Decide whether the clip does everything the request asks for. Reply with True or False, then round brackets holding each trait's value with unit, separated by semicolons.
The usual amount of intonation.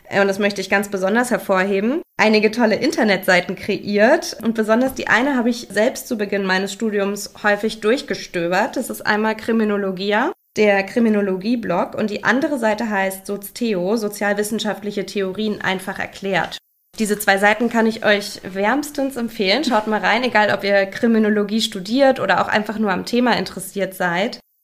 False (2.2 semitones)